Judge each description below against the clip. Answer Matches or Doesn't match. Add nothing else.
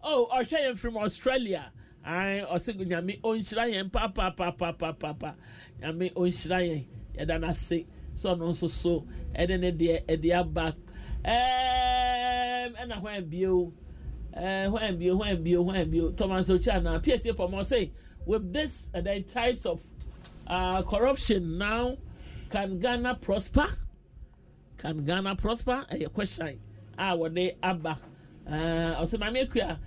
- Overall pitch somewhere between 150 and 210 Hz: Matches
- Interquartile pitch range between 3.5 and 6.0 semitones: Matches